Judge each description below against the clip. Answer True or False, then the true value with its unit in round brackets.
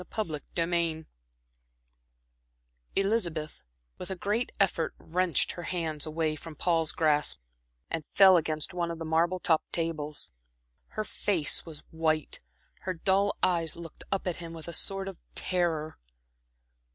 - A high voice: False (165 Hz)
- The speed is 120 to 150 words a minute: True (140 wpm)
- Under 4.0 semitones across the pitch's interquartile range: True (2.6 semitones)